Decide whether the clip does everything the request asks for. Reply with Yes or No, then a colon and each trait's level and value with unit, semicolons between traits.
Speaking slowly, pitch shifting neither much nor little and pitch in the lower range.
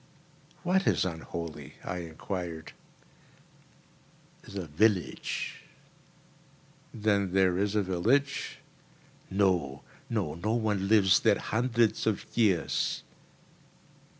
Yes: slow, 90 wpm; average, 3.9 semitones; very low, 95 Hz